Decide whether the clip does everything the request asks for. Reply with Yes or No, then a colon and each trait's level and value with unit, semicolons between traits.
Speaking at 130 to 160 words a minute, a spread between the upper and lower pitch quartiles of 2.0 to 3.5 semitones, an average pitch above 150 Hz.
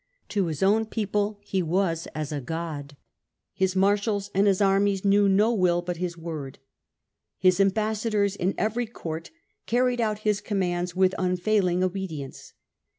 Yes: average, 155 wpm; average, 2.9 semitones; high, 190 Hz